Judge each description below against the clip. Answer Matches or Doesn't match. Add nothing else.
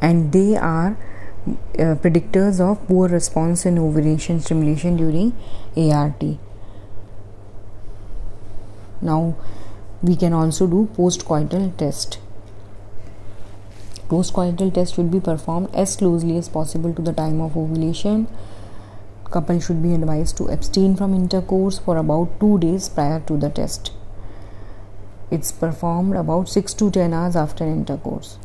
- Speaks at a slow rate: Doesn't match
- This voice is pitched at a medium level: Matches